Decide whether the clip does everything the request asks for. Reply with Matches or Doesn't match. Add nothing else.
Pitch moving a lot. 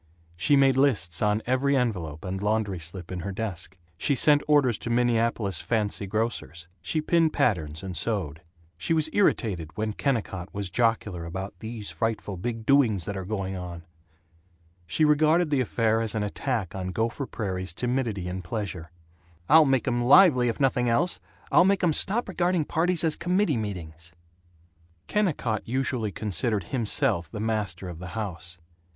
Matches